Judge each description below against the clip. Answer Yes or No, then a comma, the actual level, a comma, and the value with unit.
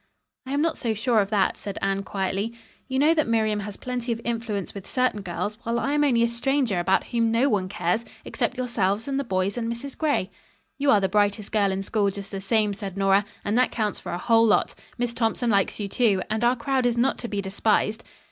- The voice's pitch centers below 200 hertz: No, high, 220 Hz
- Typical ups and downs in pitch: Yes, average, 3.5 semitones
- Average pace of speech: No, fast, 235 wpm